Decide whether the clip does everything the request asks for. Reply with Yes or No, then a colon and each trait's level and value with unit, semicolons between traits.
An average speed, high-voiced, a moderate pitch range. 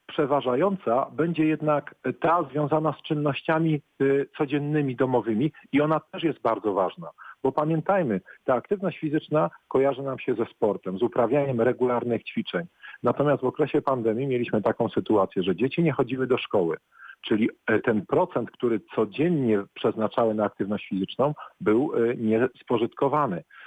No: average, 135 wpm; medium, 140 Hz; average, 4.3 semitones